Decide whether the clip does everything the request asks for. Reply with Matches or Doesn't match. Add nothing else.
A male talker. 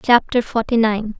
Doesn't match